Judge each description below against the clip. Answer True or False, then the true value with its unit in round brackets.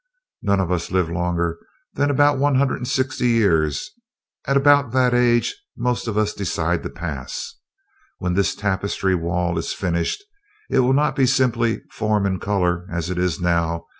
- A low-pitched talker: True (100 Hz)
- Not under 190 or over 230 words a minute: False (175 wpm)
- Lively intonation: True (6.3 semitones)